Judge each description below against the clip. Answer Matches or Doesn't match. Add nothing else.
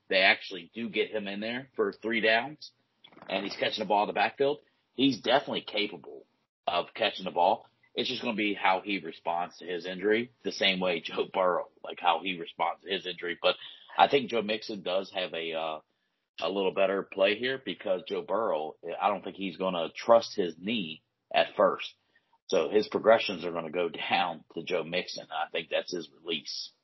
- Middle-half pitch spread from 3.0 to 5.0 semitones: Matches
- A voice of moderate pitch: Doesn't match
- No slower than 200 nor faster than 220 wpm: Matches